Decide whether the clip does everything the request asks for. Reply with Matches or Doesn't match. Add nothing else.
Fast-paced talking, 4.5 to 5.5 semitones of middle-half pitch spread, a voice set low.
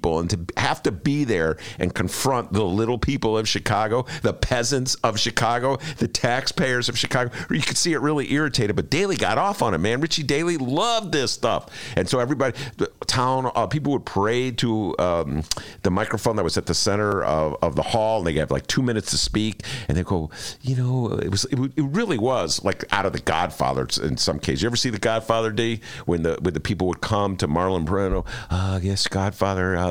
Matches